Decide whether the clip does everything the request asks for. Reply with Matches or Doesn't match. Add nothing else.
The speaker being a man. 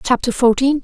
Doesn't match